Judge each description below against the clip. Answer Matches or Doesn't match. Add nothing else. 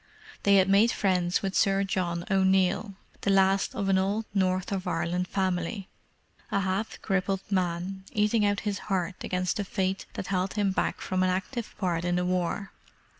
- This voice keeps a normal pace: Matches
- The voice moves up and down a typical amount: Doesn't match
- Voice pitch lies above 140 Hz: Matches